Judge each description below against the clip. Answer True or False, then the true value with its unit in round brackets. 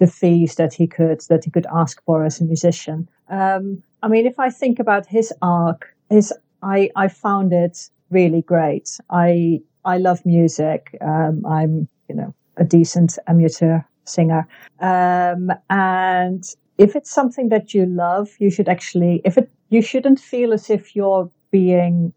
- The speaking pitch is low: False (180 Hz)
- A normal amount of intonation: True (3.0 semitones)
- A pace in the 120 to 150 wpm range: False (165 wpm)